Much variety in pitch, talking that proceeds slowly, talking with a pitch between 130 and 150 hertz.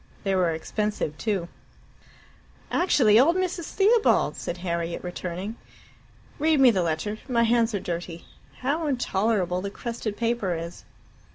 No: wide, 5.8 semitones; slow, 130 wpm; high, 210 Hz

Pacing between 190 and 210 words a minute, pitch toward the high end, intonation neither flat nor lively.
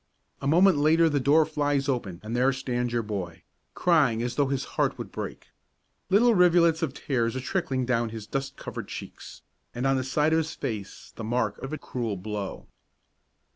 No: average, 195 wpm; low, 130 Hz; average, 5.0 semitones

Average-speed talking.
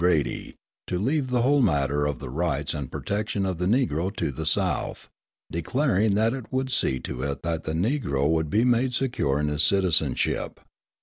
Yes: average, 185 wpm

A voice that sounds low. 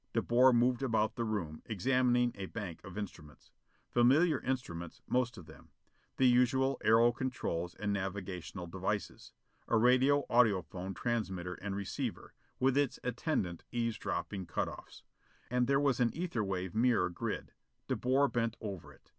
Yes: low, 115 Hz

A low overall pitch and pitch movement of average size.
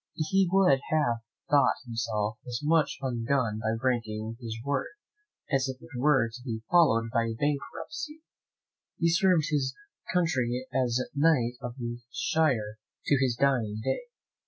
Yes: low, 130 Hz; average, 4.6 semitones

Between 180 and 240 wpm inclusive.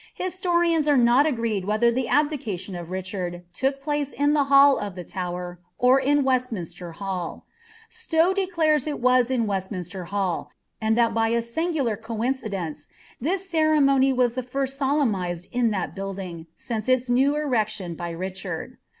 No: average, 160 wpm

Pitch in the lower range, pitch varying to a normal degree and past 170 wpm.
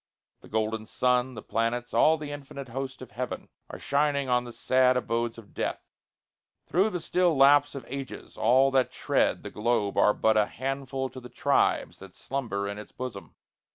Yes: low, 125 Hz; average, 3.2 semitones; average, 185 wpm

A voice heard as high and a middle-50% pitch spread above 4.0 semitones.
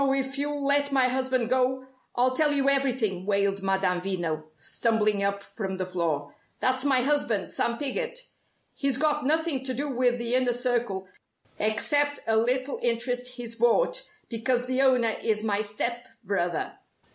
Yes: high, 245 Hz; average, 4.4 semitones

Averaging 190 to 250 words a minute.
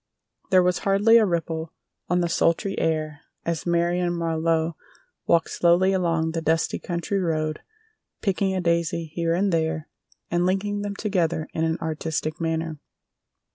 No: average, 145 wpm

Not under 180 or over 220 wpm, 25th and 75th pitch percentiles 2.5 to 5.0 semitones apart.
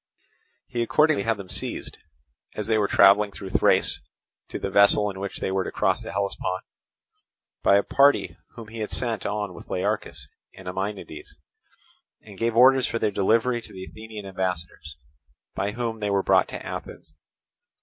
No: average, 170 wpm; average, 2.9 semitones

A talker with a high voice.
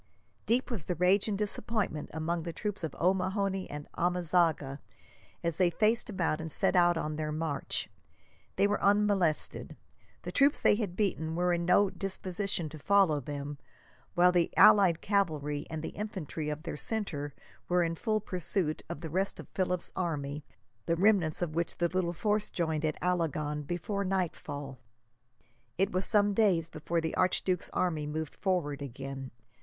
No: medium, 175 Hz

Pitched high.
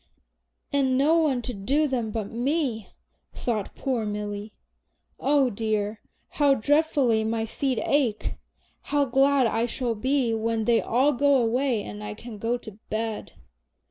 Yes: high, 240 Hz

